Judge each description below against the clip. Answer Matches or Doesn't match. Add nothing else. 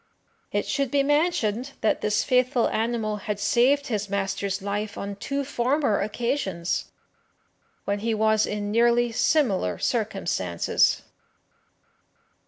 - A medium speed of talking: Doesn't match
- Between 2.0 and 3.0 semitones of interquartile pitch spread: Doesn't match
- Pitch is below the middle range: Doesn't match